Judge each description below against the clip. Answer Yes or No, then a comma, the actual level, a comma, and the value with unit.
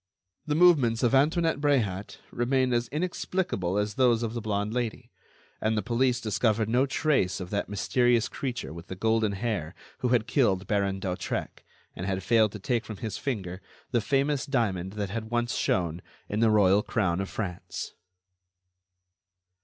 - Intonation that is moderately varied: Yes, average, 4.1 semitones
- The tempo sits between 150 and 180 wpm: Yes, average, 165 wpm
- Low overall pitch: Yes, low, 110 Hz